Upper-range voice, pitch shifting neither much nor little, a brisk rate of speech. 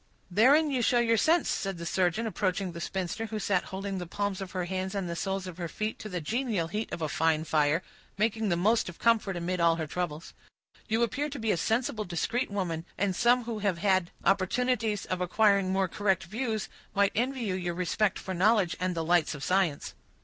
Yes: high, 195 Hz; average, 3.9 semitones; fast, 215 wpm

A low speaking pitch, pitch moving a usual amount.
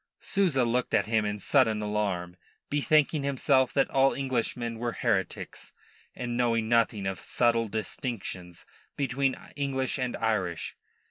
Yes: low, 120 Hz; average, 3.9 semitones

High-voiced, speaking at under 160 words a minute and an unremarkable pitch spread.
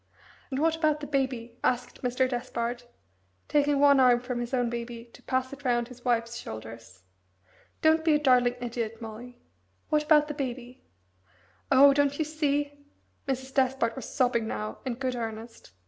No: very high, 255 Hz; average, 165 wpm; average, 3.1 semitones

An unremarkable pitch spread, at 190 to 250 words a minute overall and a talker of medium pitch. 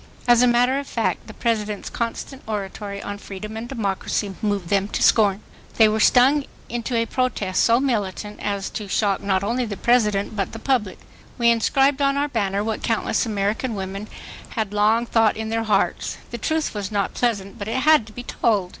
No: average, 3.0 semitones; average, 195 wpm; high, 220 Hz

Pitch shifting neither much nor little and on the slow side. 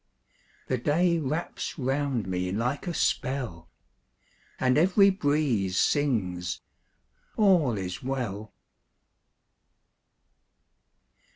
No: wide, 7.4 semitones; slow, 80 wpm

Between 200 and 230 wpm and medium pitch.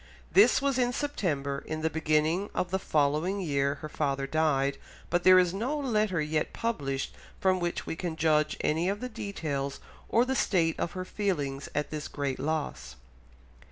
No: average, 175 wpm; medium, 160 Hz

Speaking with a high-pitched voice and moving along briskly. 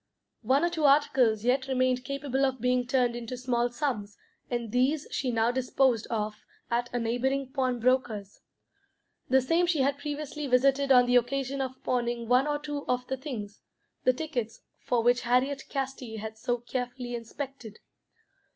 No: very high, 255 Hz; average, 160 wpm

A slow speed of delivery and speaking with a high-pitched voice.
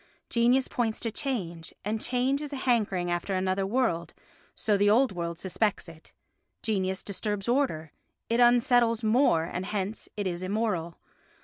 No: average, 150 wpm; high, 210 Hz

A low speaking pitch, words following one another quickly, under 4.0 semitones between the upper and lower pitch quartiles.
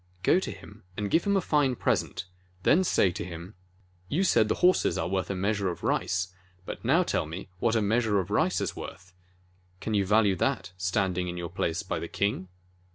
No: low, 100 Hz; fast, 210 wpm; average, 4.3 semitones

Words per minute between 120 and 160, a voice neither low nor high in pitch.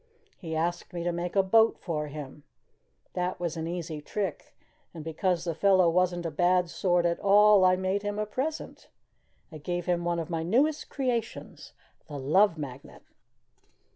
No: average, 170 wpm; medium, 175 Hz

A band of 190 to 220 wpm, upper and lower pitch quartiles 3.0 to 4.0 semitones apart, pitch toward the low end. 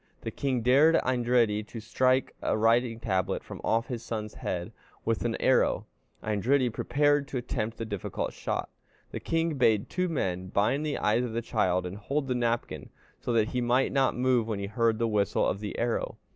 Yes: average, 195 wpm; average, 3.3 semitones; low, 115 Hz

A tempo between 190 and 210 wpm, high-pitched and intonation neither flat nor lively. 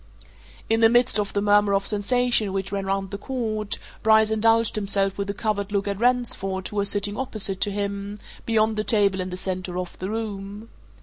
No: average, 200 wpm; high, 205 Hz; narrow, 1.9 semitones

